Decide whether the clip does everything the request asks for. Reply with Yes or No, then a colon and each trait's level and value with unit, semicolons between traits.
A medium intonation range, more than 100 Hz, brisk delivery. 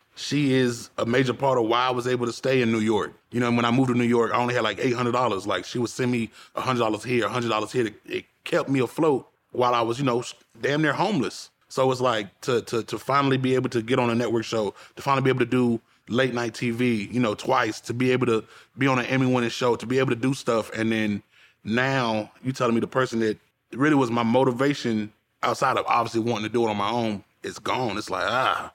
No: narrow, 2.1 semitones; low, 120 Hz; fast, 255 wpm